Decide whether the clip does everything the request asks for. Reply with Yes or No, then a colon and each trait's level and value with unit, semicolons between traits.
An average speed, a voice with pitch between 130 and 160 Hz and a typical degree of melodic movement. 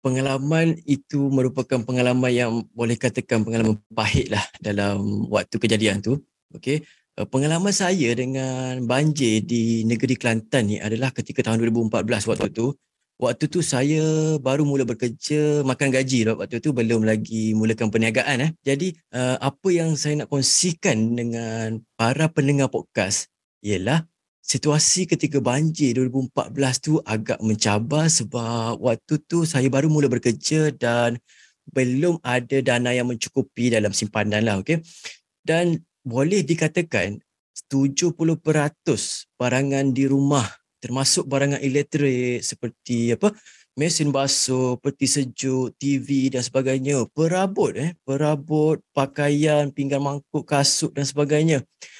Yes: average, 125 wpm; low, 135 Hz; average, 4.1 semitones